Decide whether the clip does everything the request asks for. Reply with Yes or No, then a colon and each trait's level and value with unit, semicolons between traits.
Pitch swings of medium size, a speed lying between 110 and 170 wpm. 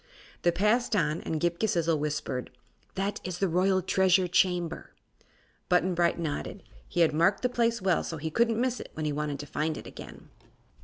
No: average, 3.4 semitones; average, 190 wpm